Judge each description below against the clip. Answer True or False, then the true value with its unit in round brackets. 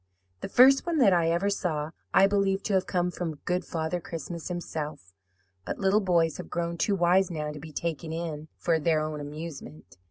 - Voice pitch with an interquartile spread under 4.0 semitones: True (3.3 semitones)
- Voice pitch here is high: False (170 Hz)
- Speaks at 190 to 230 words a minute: True (195 wpm)